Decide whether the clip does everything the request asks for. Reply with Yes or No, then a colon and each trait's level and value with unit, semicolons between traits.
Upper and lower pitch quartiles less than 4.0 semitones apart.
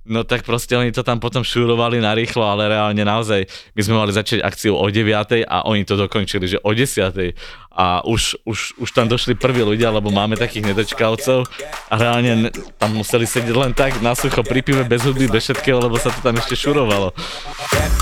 Yes: narrow, 2.6 semitones